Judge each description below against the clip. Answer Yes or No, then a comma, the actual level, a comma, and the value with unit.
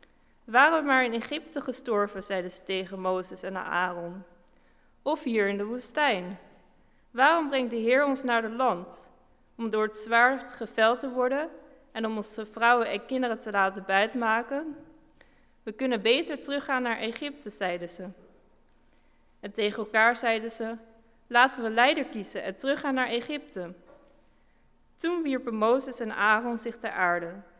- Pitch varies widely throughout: No, average, 4.3 semitones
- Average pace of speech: Yes, average, 150 wpm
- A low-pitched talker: No, high, 230 Hz